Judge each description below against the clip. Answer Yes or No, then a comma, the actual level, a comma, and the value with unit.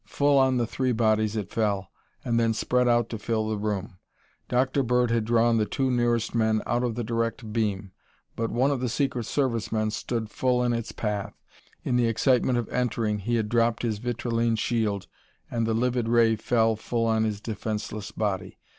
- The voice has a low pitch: Yes, low, 115 Hz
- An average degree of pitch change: No, narrow, 1.9 semitones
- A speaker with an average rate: Yes, average, 195 wpm